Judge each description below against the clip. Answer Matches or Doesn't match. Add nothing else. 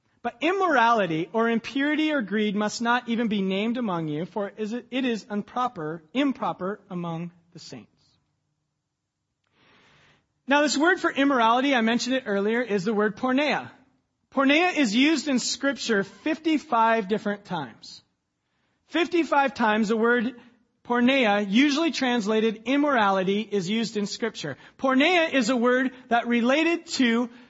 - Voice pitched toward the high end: Matches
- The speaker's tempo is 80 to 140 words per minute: Matches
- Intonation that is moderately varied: Matches